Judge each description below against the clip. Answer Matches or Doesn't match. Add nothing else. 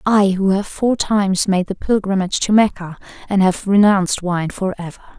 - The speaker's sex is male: Doesn't match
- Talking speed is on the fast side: Doesn't match